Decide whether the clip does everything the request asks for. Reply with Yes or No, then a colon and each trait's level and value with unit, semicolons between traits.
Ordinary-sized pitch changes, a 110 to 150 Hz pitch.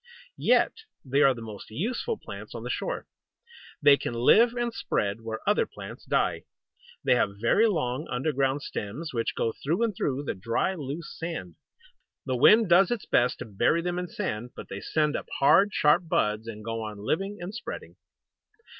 No: wide, 7.8 semitones; medium, 140 Hz